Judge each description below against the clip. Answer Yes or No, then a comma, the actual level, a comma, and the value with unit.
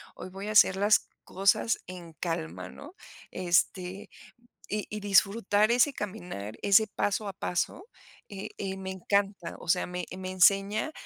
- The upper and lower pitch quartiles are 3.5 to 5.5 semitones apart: No, narrow, 2.5 semitones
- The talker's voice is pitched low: No, high, 195 Hz